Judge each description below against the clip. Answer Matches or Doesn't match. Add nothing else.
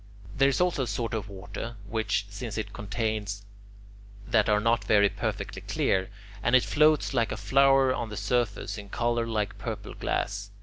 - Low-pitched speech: Matches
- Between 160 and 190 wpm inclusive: Matches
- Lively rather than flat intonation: Doesn't match